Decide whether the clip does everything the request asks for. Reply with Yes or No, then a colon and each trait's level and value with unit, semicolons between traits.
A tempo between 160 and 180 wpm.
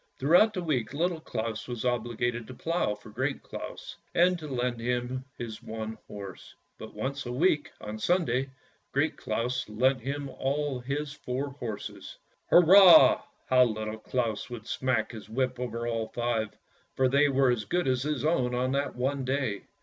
Yes: average, 175 wpm